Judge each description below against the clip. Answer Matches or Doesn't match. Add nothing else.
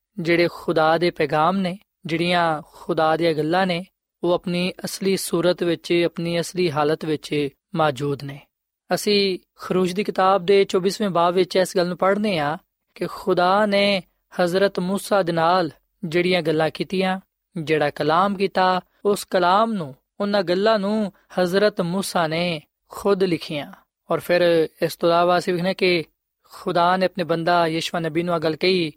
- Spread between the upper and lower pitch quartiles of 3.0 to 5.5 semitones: Doesn't match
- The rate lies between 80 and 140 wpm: Matches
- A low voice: Doesn't match